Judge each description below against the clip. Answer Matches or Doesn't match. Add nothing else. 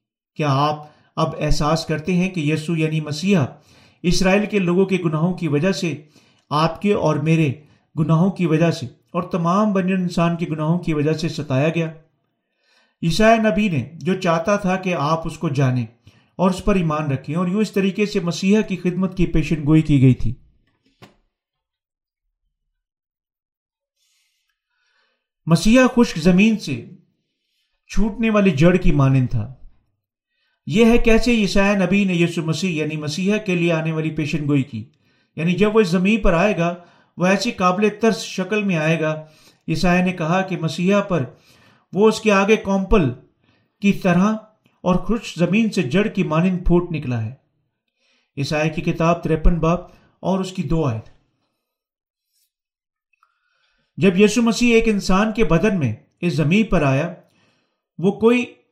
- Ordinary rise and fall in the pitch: Matches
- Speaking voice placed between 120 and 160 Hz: Doesn't match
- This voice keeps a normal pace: Matches